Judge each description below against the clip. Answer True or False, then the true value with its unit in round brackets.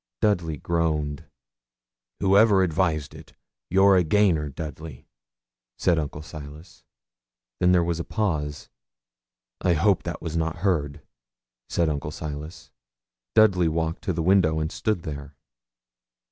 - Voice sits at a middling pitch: False (80 Hz)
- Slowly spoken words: True (125 wpm)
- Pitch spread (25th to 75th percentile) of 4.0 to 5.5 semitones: False (3.2 semitones)